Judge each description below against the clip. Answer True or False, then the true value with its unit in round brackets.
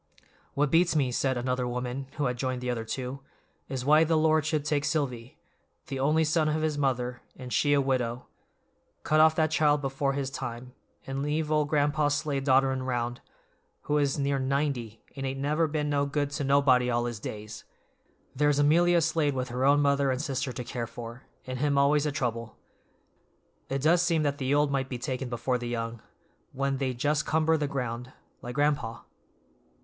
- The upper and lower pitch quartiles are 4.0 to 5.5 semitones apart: False (2.9 semitones)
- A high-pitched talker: False (140 Hz)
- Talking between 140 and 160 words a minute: False (185 wpm)